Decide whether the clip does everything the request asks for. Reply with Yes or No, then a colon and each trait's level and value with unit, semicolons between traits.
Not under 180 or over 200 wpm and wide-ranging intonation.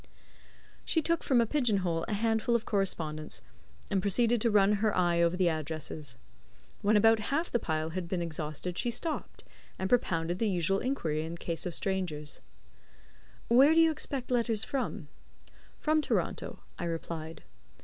No: average, 165 wpm; wide, 6.1 semitones